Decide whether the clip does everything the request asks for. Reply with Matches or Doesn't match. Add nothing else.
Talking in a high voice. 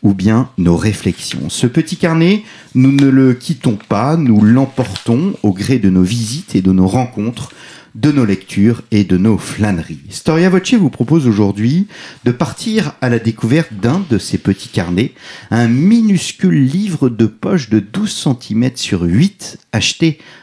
Doesn't match